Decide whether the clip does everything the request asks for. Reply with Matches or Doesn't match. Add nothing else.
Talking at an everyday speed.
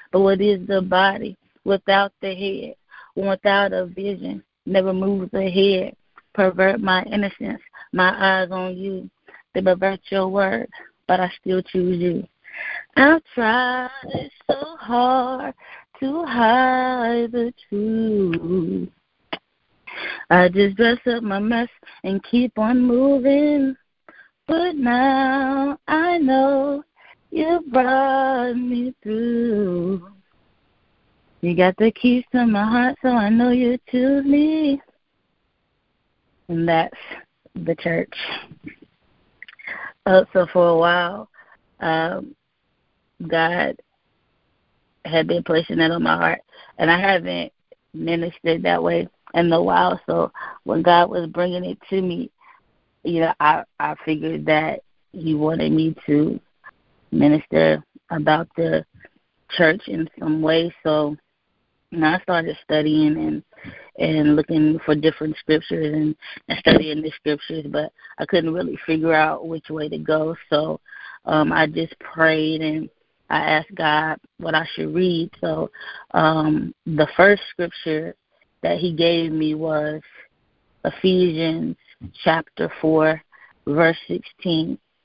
Doesn't match